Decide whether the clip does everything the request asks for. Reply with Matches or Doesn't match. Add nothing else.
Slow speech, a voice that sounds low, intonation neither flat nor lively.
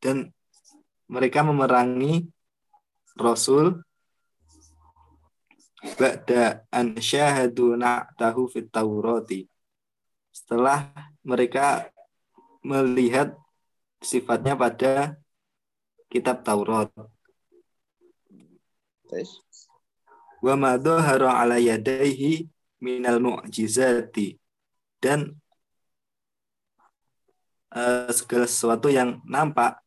Matches